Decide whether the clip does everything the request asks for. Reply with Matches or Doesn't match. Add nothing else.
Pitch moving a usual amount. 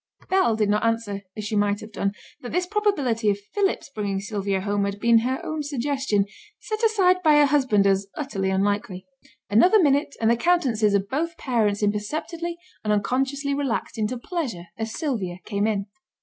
Doesn't match